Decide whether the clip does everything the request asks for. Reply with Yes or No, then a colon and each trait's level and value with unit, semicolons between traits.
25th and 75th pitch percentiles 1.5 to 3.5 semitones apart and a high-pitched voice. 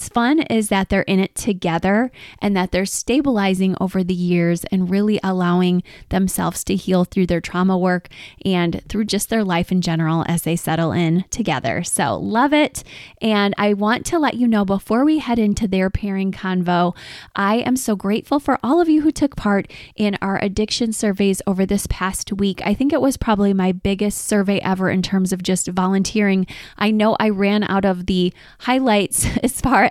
Yes: average, 2.7 semitones; high, 195 Hz